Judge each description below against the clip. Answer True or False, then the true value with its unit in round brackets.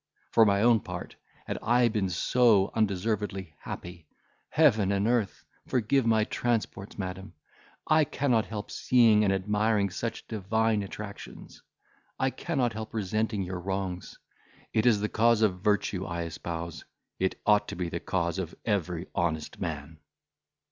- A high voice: False (105 Hz)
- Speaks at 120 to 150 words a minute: True (140 wpm)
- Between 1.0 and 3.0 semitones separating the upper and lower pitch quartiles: False (3.4 semitones)